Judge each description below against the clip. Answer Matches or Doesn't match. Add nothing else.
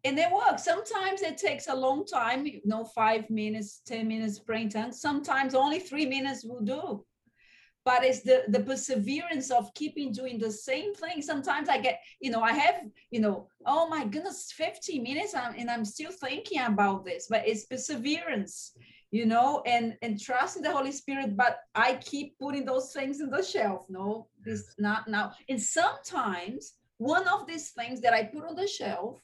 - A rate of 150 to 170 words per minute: Doesn't match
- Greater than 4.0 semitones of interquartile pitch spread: Matches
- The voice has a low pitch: Doesn't match